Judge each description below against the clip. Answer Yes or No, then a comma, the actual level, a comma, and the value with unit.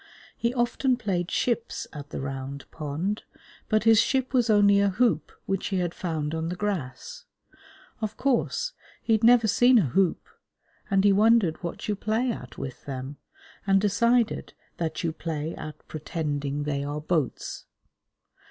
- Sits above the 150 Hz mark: Yes, high, 190 Hz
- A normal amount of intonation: No, wide, 6.9 semitones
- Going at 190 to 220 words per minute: No, average, 160 wpm